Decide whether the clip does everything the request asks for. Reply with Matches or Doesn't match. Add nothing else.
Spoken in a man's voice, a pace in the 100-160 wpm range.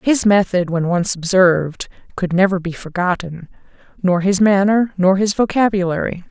Doesn't match